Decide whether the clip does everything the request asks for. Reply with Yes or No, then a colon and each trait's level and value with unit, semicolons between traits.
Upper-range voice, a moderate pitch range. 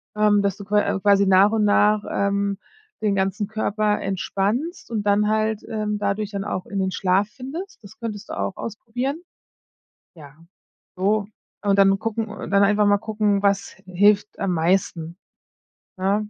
No: high, 205 Hz; narrow, 1.5 semitones